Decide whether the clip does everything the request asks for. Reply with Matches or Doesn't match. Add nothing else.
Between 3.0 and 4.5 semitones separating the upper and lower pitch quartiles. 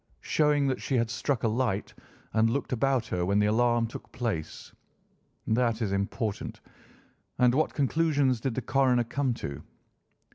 Matches